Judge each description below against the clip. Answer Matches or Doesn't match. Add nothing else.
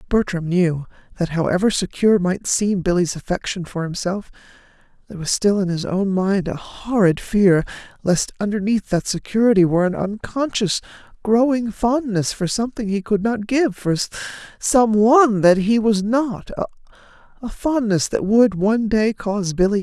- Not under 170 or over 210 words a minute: Doesn't match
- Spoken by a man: Doesn't match